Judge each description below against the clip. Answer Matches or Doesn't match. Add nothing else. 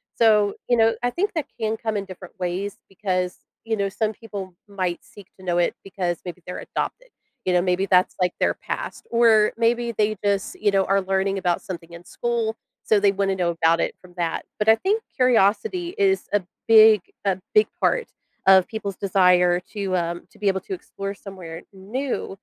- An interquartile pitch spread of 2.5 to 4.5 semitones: Matches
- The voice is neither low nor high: Doesn't match